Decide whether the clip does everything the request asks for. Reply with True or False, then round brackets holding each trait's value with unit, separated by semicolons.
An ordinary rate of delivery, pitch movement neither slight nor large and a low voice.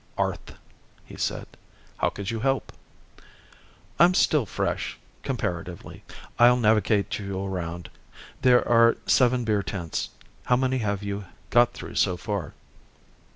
False (125 wpm; 4.0 semitones; 105 Hz)